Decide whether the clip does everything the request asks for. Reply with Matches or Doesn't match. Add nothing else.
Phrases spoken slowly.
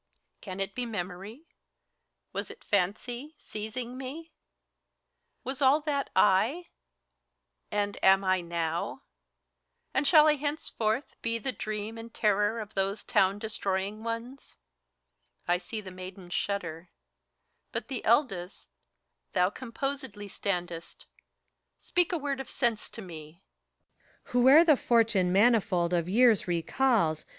Matches